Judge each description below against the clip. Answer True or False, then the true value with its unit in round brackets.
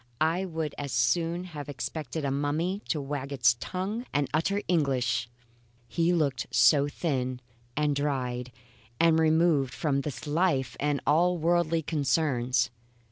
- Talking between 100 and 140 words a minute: True (135 wpm)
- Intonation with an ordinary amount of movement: True (3.7 semitones)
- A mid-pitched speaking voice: True (145 Hz)